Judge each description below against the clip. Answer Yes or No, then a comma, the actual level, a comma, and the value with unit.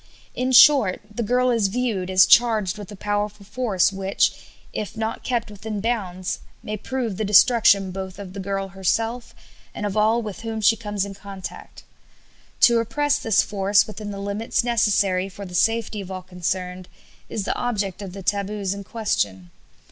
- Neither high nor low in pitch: No, high, 205 Hz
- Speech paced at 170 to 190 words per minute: Yes, average, 175 wpm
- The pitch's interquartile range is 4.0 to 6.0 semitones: No, average, 2.8 semitones